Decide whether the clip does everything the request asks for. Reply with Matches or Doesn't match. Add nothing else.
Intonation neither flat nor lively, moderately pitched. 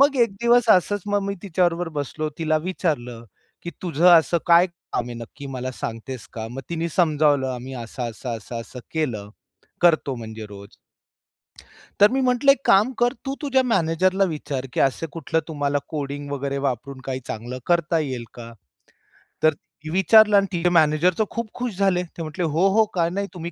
Doesn't match